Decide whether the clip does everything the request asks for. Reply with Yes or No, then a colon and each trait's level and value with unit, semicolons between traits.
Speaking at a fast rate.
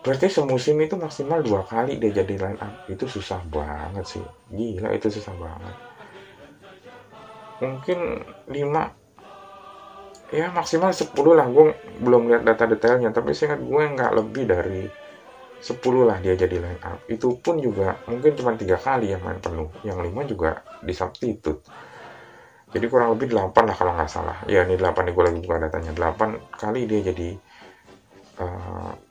Yes: fast, 160 wpm